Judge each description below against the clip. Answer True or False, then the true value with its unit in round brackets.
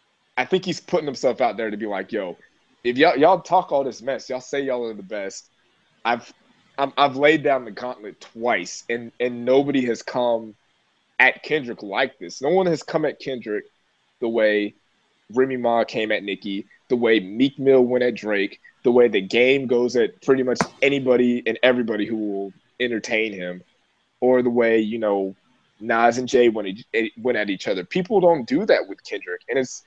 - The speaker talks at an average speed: True (195 wpm)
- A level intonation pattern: False (3.5 semitones)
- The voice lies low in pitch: True (125 Hz)